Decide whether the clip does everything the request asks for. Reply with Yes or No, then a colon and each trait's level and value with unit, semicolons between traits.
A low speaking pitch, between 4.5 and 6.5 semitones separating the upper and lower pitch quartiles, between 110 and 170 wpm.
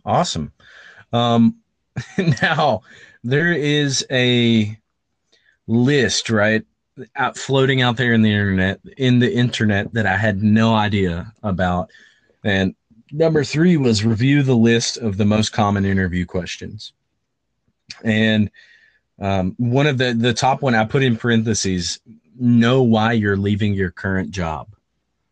No: low, 115 Hz; average, 3.7 semitones; slow, 135 wpm